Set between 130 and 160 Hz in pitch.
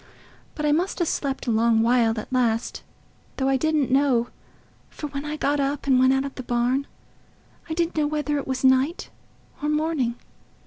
No: very high, 275 Hz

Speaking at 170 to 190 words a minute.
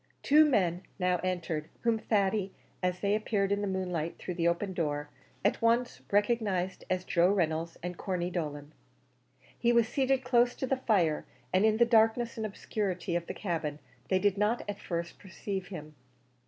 Yes: average, 175 wpm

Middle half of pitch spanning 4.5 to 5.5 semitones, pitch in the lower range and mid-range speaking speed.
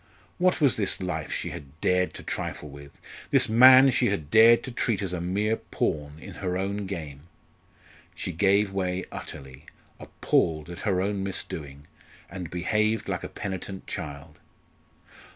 Yes: average, 5.0 semitones; very low, 95 Hz; average, 155 wpm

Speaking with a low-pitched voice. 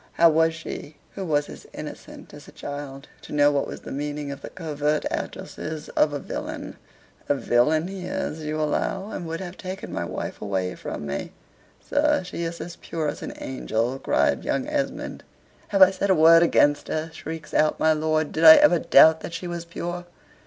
No: medium, 160 Hz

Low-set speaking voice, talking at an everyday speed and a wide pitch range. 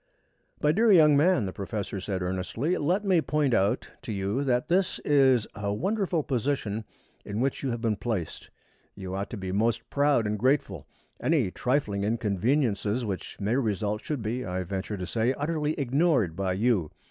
Yes: low, 115 Hz; average, 175 wpm; wide, 6.2 semitones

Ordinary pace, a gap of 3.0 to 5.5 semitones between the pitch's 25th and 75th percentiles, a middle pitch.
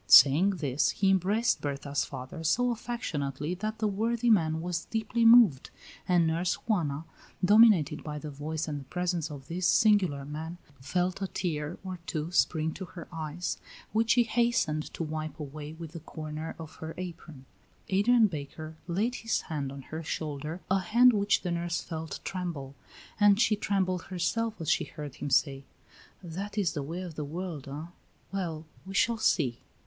Yes: average, 175 wpm; average, 4.6 semitones; medium, 170 Hz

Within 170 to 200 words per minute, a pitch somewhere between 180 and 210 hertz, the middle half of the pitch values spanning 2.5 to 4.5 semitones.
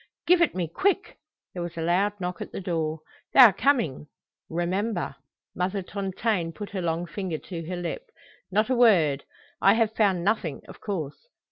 Yes: average, 175 wpm; medium, 185 Hz; average, 4.2 semitones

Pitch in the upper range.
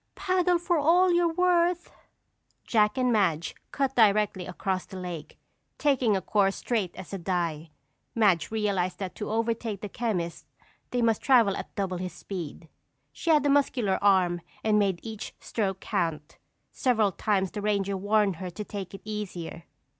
Yes: high, 205 Hz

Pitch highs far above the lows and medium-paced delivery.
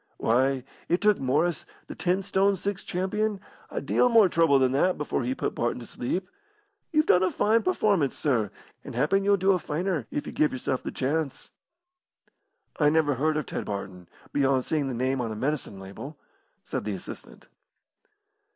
Yes: wide, 6.3 semitones; average, 180 wpm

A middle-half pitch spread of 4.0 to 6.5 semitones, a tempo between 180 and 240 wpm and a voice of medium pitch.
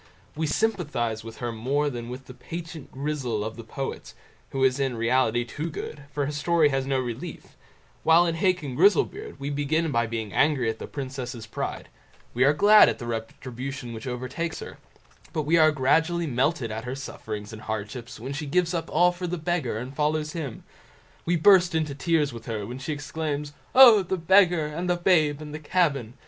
Yes: average, 5.0 semitones; average, 195 wpm; medium, 145 Hz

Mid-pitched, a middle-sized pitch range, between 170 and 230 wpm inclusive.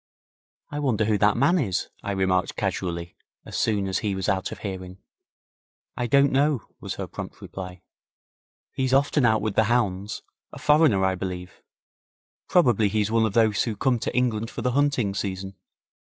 No: low, 110 Hz; average, 4.7 semitones; average, 175 wpm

